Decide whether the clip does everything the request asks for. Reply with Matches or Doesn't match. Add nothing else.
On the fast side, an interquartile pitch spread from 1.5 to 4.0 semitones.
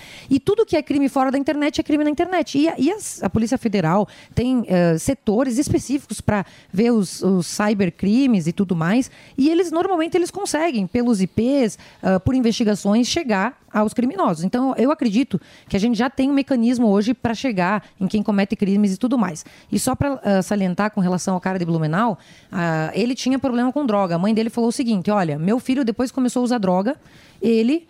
Doesn't match